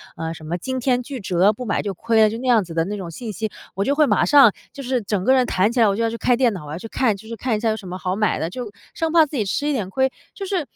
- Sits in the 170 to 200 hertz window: No, high, 220 Hz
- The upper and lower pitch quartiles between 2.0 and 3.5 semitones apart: No, average, 5.2 semitones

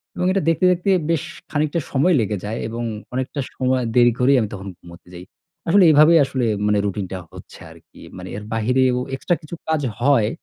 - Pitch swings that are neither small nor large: No, wide, 6.1 semitones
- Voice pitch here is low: Yes, low, 130 Hz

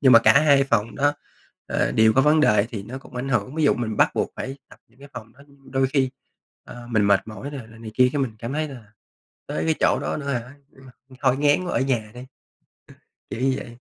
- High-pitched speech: No, low, 130 Hz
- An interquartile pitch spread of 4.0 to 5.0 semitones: No, average, 3.5 semitones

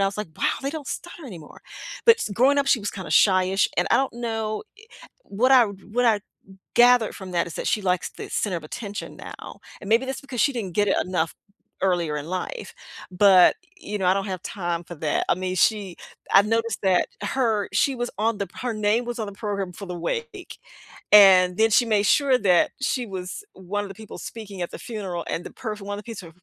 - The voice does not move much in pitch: No, average, 4.0 semitones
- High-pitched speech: Yes, high, 205 Hz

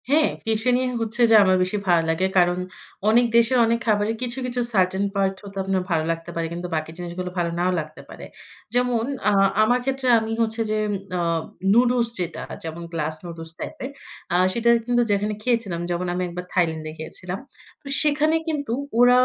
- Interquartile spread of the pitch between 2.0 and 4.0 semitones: No, wide, 5.5 semitones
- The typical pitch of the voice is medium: No, high, 200 Hz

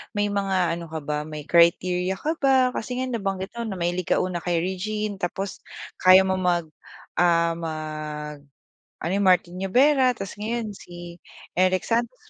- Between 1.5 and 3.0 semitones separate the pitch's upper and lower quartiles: No, average, 3.4 semitones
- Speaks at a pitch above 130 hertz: Yes, medium, 185 Hz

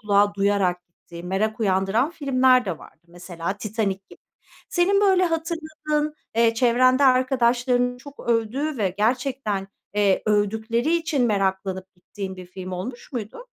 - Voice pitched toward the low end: No, high, 225 Hz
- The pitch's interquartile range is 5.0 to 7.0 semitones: Yes, average, 5.3 semitones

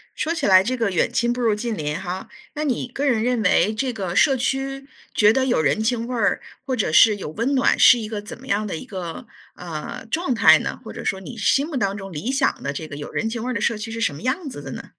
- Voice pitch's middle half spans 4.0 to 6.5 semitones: Yes, average, 5.0 semitones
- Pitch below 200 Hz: No, high, 225 Hz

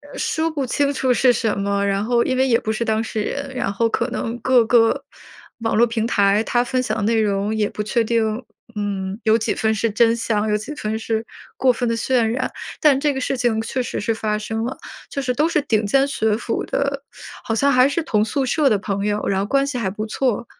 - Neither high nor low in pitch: No, high, 230 Hz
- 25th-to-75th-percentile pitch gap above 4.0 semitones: No, average, 3.2 semitones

